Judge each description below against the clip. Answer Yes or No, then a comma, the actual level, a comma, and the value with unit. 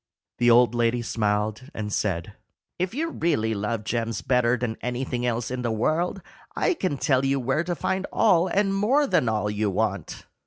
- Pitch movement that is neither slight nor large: No, wide, 7.3 semitones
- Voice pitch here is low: Yes, low, 120 Hz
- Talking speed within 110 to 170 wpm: No, average, 185 wpm